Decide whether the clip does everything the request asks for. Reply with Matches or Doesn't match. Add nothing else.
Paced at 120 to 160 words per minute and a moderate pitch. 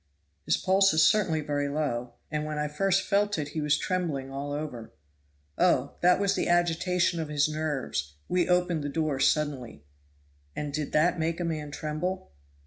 Doesn't match